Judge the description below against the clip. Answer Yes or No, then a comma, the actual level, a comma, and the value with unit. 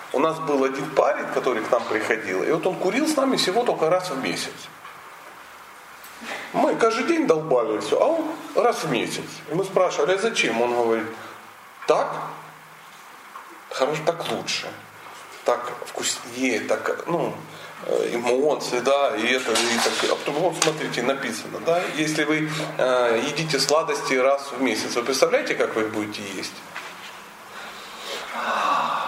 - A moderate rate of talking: Yes, average, 140 wpm